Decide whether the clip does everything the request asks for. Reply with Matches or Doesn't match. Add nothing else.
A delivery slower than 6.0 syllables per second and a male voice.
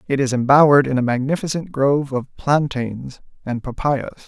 Matches